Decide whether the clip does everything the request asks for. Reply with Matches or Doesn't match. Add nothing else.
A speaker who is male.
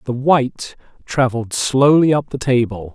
Matches